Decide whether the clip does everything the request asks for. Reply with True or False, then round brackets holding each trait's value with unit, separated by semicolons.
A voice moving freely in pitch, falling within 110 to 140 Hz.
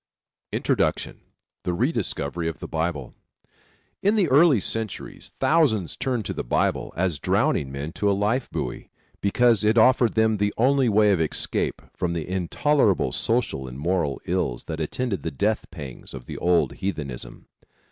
False (6.6 semitones; 100 Hz)